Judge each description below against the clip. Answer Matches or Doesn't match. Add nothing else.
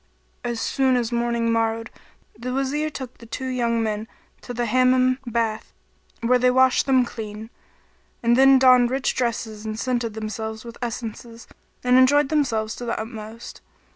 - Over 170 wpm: Doesn't match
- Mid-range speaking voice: Doesn't match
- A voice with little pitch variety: Matches